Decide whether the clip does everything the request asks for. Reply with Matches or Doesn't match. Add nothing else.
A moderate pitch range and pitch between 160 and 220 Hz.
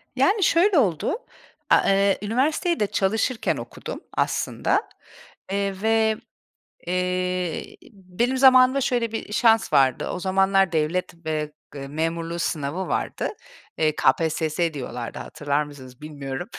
Doesn't match